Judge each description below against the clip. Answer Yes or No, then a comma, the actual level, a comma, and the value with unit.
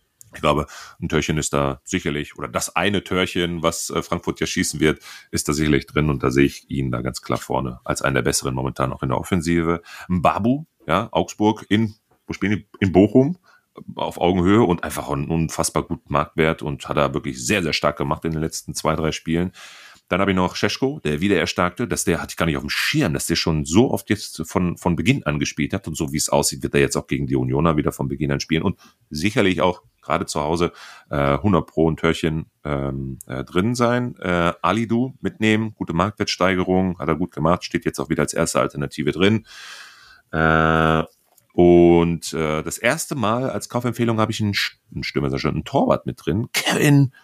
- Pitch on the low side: Yes, very low, 85 Hz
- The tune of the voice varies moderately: Yes, average, 4.5 semitones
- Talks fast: Yes, fast, 200 wpm